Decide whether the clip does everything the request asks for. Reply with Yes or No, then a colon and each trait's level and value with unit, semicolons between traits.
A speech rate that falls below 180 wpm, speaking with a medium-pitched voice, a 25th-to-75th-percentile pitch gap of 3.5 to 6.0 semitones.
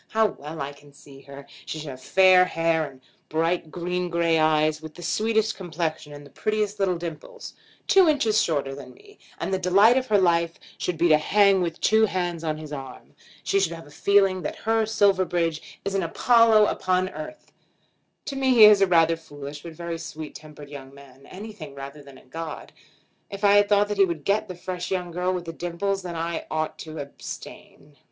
No: fast, 205 wpm; medium, 170 Hz; average, 4.3 semitones